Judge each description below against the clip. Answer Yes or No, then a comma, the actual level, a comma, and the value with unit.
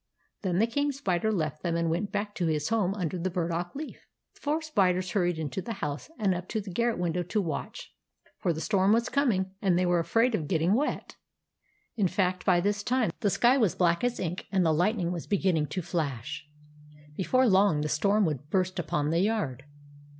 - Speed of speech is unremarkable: No, fast, 210 wpm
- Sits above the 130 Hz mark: Yes, medium, 185 Hz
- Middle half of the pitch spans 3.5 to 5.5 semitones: Yes, average, 4.1 semitones